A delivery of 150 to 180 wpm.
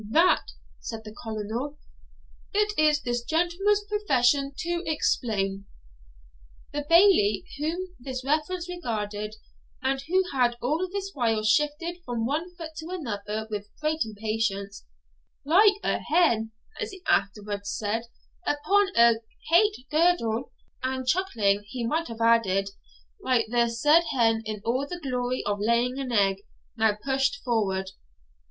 No: slow, 135 wpm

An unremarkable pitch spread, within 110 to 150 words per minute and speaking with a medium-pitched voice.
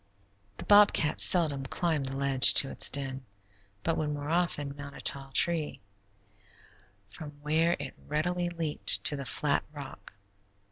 Yes: average, 3.1 semitones; average, 145 wpm; medium, 150 Hz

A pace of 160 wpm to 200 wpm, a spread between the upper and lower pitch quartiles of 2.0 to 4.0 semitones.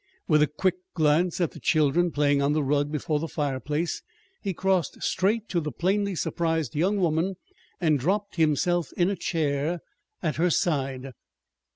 Yes: average, 165 wpm; average, 3.3 semitones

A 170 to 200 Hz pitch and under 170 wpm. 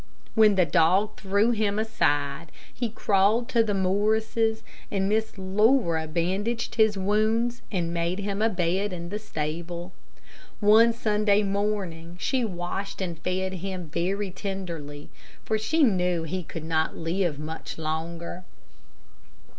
Yes: high, 190 Hz; slow, 135 wpm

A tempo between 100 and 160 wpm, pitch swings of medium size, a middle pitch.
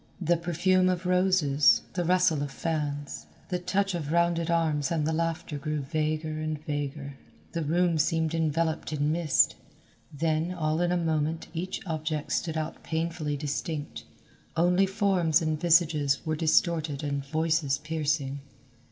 No: average, 145 wpm; narrow, 2.3 semitones; medium, 160 Hz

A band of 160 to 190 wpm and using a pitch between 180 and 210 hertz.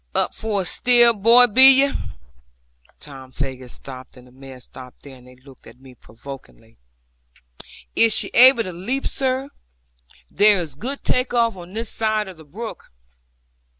Yes: average, 165 wpm; high, 190 Hz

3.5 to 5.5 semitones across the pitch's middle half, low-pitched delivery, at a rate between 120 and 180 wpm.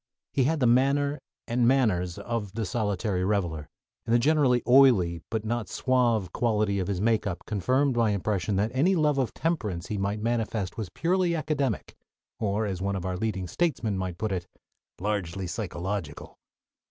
Yes: average, 4.9 semitones; low, 110 Hz; average, 165 wpm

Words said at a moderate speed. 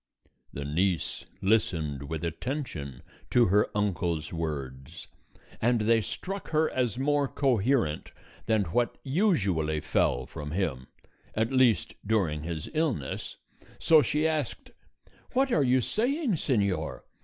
No: slow, 120 wpm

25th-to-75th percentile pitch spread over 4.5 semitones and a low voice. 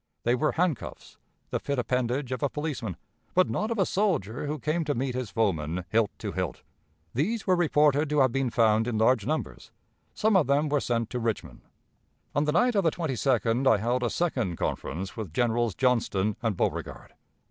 Yes: average, 5.1 semitones; low, 130 Hz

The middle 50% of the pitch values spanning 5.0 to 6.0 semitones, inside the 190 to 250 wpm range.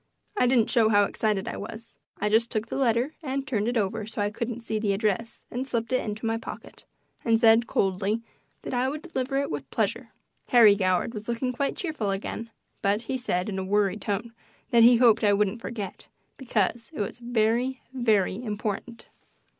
No: average, 2.7 semitones; average, 195 wpm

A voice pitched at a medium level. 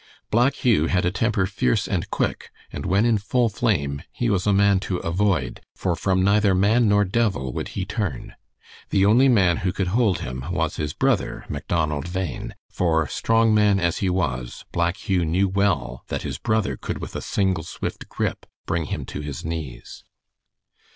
No: very low, 95 Hz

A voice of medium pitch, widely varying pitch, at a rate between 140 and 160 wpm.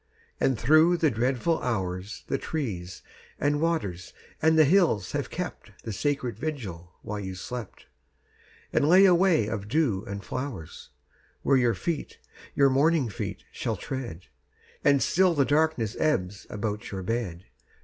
No: low, 125 Hz; wide, 7.5 semitones; average, 150 wpm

